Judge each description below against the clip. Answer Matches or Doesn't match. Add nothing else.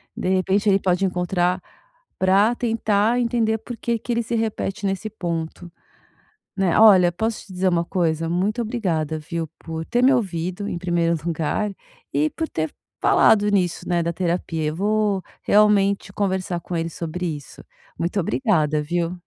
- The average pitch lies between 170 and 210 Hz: Matches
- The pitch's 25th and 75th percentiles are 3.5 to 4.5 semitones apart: Matches